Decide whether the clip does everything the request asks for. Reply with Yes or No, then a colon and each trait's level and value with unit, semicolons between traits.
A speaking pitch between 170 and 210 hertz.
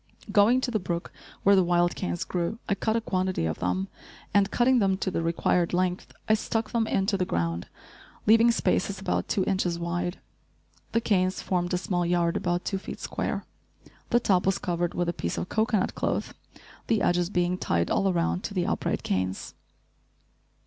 Yes: medium, 185 Hz